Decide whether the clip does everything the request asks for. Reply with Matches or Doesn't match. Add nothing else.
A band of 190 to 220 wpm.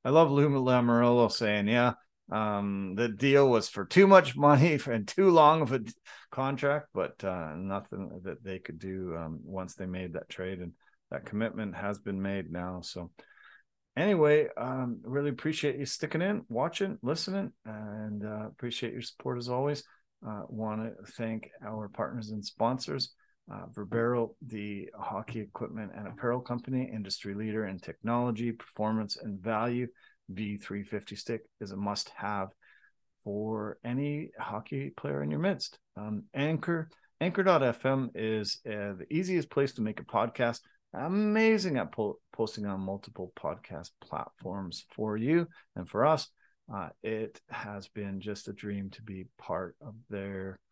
Doesn't match